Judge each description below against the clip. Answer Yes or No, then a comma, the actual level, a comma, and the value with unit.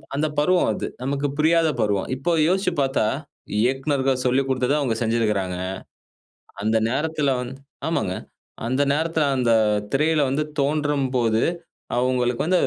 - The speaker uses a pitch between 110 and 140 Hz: Yes, low, 135 Hz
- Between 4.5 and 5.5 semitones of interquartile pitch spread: No, average, 3.7 semitones